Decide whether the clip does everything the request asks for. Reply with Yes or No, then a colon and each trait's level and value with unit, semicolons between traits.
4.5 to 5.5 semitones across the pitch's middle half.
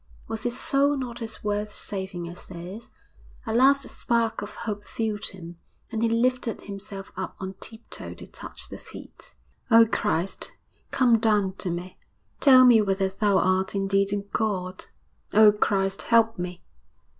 No: average, 3.2 semitones